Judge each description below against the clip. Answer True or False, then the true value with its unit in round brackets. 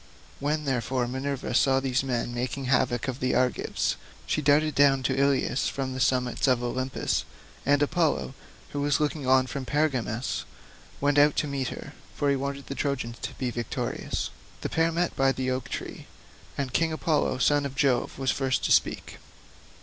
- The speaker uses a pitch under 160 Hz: True (135 Hz)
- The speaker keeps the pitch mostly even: True (2.0 semitones)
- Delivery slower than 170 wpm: False (180 wpm)